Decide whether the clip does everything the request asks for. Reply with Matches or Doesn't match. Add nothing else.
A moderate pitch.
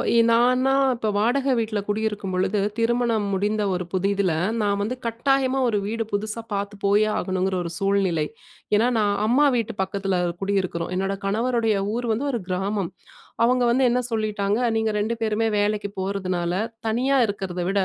Doesn't match